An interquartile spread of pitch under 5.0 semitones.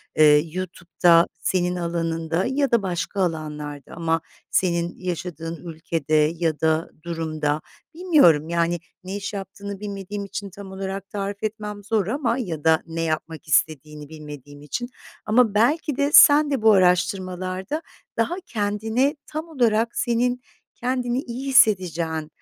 No: wide, 5.4 semitones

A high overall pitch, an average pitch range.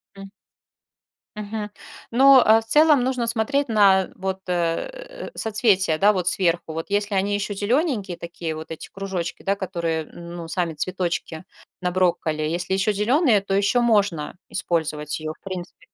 Yes: high, 195 Hz; average, 4.2 semitones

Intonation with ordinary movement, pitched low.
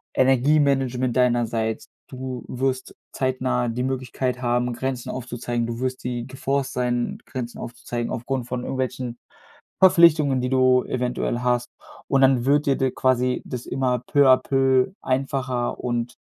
No: narrow, 1.4 semitones; low, 125 Hz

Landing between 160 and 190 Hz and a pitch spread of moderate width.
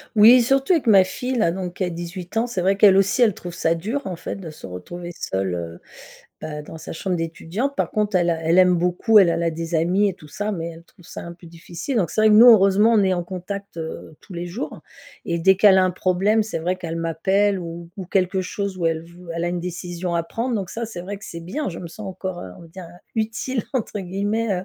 Yes: medium, 185 Hz; average, 3.5 semitones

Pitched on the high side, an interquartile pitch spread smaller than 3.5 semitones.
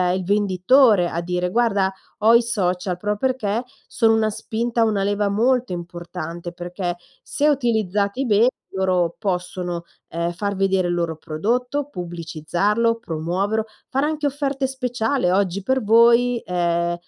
No: high, 200 Hz; average, 4.9 semitones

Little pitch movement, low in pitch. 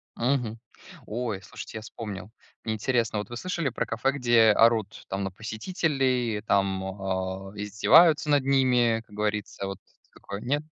No: average, 3.8 semitones; low, 110 Hz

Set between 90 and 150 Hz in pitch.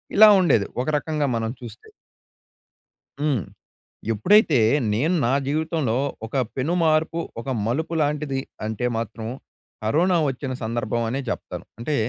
Yes: medium, 140 Hz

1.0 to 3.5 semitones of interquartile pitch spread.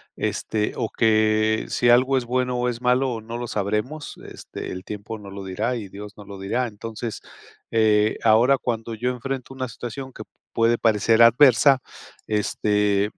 Yes: average, 2.8 semitones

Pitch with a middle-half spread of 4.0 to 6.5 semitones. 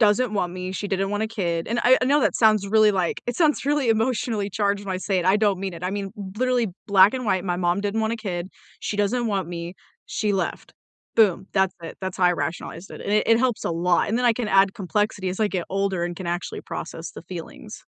No: average, 3.2 semitones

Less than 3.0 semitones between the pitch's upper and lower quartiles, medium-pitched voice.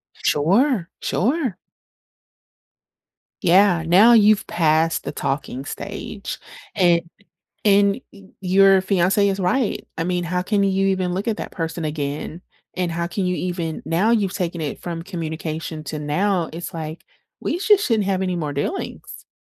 No: average, 3.4 semitones; medium, 180 Hz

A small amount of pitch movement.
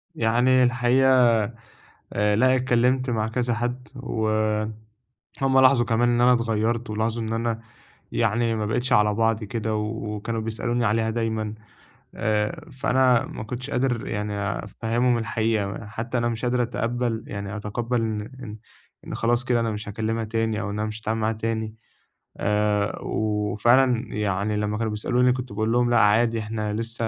Yes: narrow, 2.1 semitones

